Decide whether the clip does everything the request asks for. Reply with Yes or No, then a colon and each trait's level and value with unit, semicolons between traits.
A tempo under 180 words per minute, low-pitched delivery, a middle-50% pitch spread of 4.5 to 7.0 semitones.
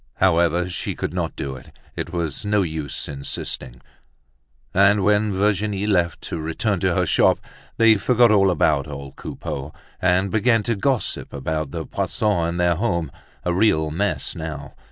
Yes: average, 160 wpm; very low, 90 Hz; average, 4.8 semitones